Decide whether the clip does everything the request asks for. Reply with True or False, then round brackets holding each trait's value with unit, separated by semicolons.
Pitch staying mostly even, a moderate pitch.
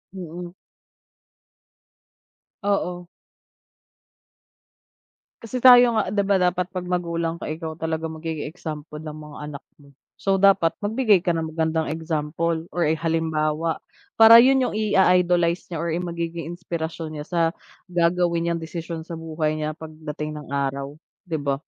True (2.3 semitones; 165 Hz)